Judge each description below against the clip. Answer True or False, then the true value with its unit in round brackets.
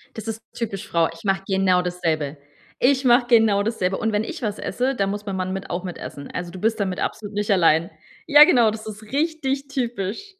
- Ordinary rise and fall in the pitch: True (4.3 semitones)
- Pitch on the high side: True (205 Hz)